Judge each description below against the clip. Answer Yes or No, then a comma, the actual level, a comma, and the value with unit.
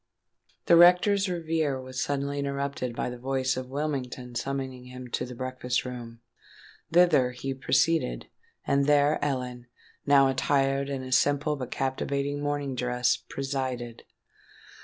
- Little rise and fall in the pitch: Yes, narrow, 2.1 semitones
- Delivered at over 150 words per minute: No, slow, 135 wpm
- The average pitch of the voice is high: No, low, 135 Hz